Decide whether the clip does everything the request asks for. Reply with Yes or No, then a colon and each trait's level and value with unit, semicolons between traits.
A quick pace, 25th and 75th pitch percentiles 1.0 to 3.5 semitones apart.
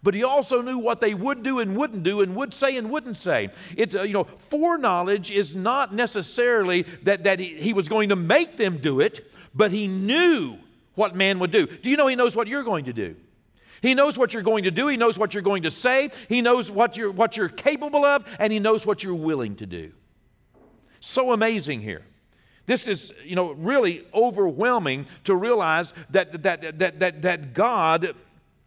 No: fast, 210 wpm; average, 5.2 semitones